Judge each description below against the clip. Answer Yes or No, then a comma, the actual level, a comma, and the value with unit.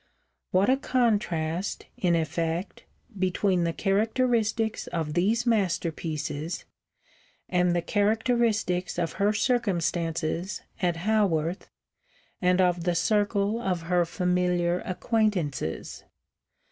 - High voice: No, medium, 180 Hz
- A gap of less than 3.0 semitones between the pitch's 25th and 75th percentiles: No, average, 3.8 semitones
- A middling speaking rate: No, slow, 100 wpm